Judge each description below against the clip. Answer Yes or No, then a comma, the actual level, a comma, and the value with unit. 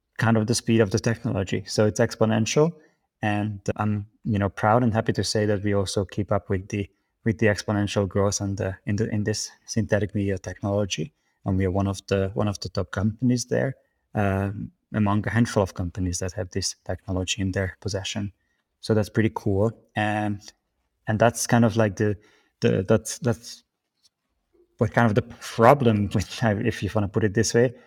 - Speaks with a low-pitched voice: Yes, low, 105 Hz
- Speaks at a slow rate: No, average, 200 wpm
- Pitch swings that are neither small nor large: No, narrow, 2.3 semitones